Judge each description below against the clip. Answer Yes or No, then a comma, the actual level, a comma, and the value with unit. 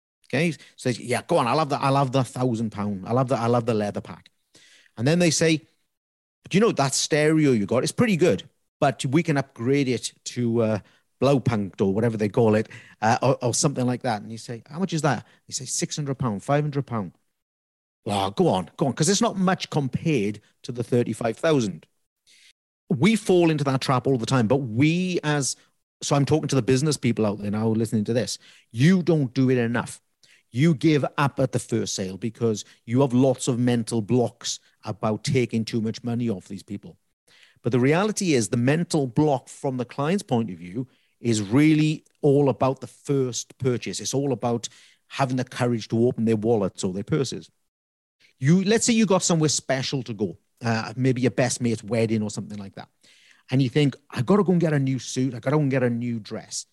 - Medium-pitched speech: No, low, 130 Hz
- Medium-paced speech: No, fast, 220 wpm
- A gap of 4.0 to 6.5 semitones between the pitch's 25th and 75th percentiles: Yes, average, 4.4 semitones